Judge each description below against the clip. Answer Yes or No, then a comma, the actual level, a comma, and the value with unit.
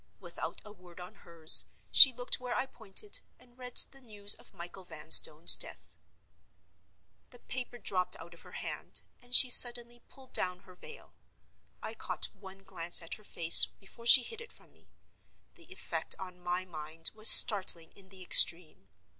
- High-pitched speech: Yes, high, 195 Hz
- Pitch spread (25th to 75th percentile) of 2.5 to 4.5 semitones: No, wide, 5.5 semitones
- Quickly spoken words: No, average, 170 wpm